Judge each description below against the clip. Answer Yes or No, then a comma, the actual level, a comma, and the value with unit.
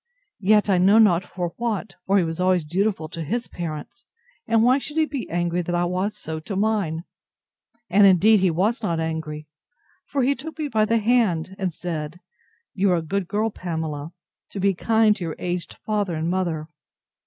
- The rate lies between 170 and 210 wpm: Yes, average, 195 wpm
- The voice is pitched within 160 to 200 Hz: Yes, medium, 185 Hz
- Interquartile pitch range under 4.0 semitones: No, average, 4.4 semitones